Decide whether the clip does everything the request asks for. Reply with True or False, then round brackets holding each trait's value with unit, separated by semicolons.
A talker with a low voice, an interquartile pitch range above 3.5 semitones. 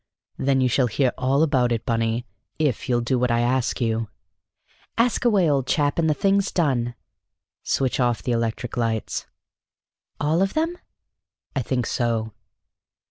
True (125 Hz; 3.9 semitones)